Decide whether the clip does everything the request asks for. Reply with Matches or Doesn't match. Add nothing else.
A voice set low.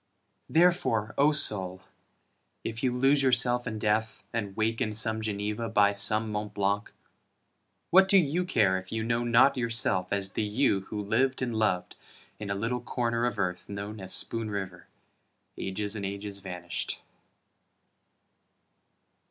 Matches